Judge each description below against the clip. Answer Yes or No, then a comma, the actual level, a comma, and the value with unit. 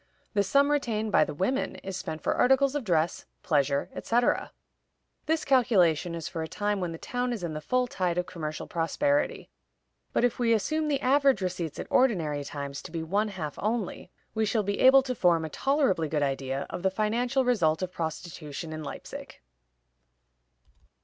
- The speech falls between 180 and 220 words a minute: Yes, average, 185 wpm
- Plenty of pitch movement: Yes, wide, 7.5 semitones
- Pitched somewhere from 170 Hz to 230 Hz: Yes, high, 190 Hz